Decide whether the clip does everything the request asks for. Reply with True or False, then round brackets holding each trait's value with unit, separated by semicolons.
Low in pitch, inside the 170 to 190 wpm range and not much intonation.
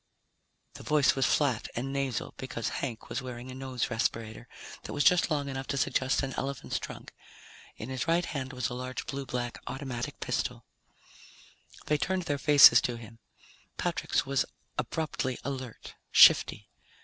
False (130 Hz; 160 wpm; 2.3 semitones)